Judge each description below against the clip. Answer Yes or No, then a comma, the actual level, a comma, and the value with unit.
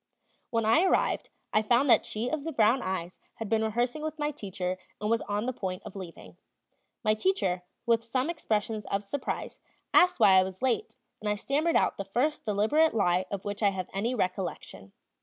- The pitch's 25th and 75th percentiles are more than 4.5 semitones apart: Yes, average, 4.9 semitones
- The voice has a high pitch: Yes, high, 220 Hz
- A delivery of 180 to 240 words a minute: Yes, average, 195 wpm